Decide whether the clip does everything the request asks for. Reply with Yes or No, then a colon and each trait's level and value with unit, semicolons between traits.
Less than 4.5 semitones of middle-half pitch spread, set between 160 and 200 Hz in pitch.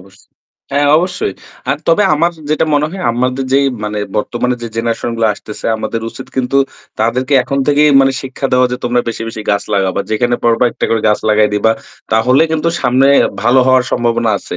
No: average, 3.2 semitones; low, 125 Hz